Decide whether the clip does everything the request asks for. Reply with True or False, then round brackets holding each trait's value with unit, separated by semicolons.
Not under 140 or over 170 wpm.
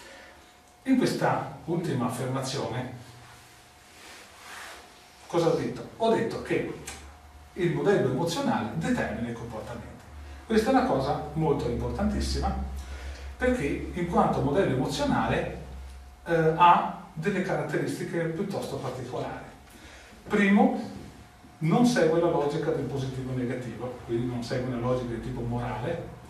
False (115 wpm)